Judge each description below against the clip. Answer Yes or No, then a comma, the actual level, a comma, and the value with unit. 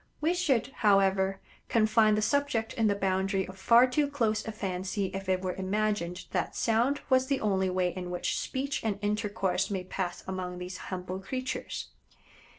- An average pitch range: Yes, average, 3.4 semitones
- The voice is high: Yes, high, 200 Hz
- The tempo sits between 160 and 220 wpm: Yes, average, 170 wpm